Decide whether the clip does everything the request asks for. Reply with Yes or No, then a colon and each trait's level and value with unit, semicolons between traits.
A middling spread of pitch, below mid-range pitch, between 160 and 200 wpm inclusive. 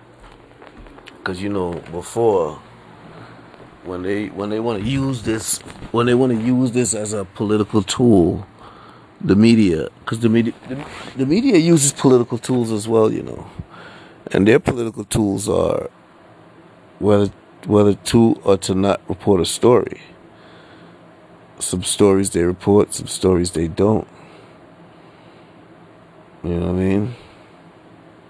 No: average, 3.4 semitones; low, 105 Hz; slow, 135 wpm